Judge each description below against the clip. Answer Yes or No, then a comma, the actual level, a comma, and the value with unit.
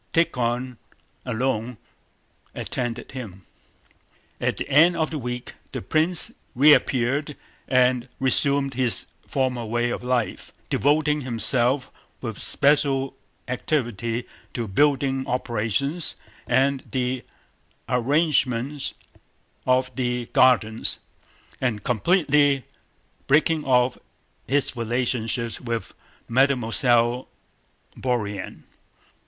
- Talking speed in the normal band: No, slow, 90 wpm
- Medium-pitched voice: No, low, 130 Hz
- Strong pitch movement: No, average, 2.7 semitones